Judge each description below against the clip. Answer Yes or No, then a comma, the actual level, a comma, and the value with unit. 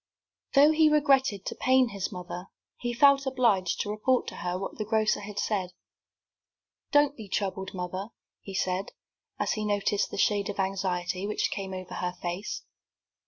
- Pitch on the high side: Yes, high, 205 Hz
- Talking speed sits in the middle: Yes, average, 165 wpm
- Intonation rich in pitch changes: No, average, 4.5 semitones